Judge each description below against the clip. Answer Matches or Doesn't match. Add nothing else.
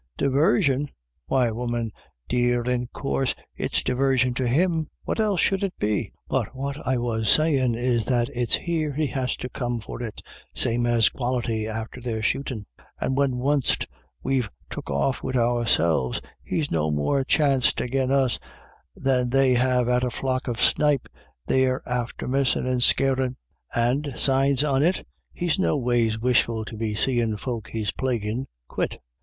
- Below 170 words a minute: Matches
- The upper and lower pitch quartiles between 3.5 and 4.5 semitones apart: Doesn't match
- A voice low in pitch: Matches